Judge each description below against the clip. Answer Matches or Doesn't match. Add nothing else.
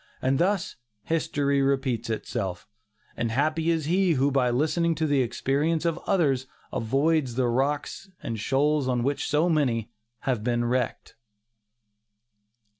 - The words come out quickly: Doesn't match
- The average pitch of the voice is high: Doesn't match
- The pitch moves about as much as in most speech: Matches